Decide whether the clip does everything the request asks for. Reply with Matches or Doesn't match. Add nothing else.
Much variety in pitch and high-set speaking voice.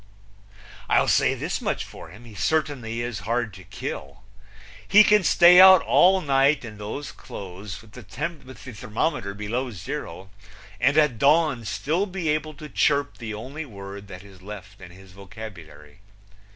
Doesn't match